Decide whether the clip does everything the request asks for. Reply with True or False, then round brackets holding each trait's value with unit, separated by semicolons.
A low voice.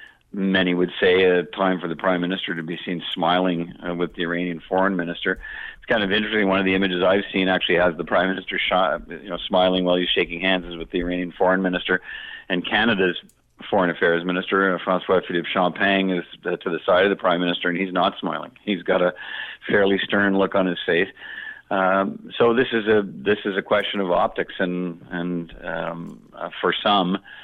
True (90 Hz)